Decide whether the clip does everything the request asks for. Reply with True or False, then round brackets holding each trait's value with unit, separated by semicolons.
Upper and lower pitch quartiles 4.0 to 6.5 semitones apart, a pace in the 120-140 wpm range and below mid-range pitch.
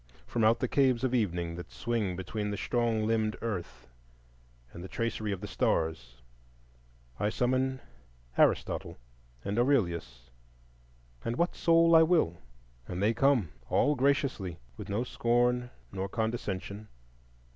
True (4.8 semitones; 135 wpm; 110 Hz)